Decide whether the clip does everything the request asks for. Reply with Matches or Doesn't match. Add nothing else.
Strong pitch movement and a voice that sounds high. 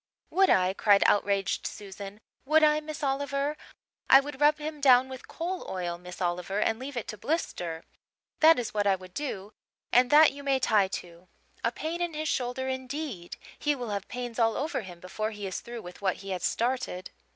Matches